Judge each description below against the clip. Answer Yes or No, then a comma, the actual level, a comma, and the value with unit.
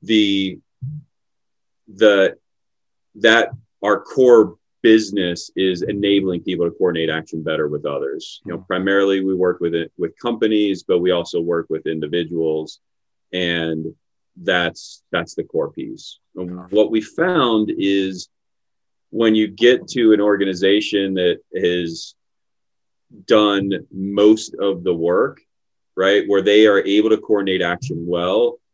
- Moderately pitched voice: No, low, 100 Hz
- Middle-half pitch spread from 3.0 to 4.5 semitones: Yes, average, 3.6 semitones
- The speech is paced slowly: Yes, slow, 130 wpm